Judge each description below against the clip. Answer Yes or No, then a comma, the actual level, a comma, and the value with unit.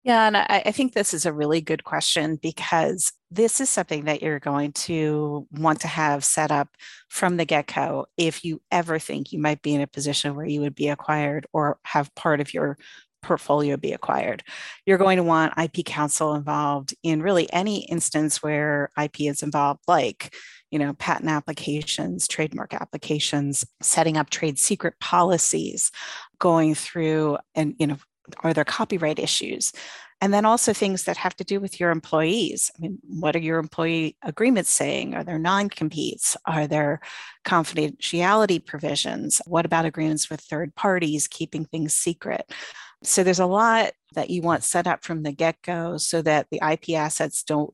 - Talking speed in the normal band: Yes, average, 175 wpm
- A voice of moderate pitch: Yes, medium, 160 Hz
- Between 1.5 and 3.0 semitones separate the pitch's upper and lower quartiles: Yes, average, 2.7 semitones